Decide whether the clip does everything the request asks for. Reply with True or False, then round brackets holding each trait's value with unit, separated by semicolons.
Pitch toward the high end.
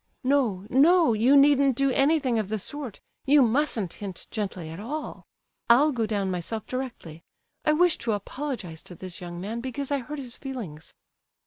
True (240 Hz)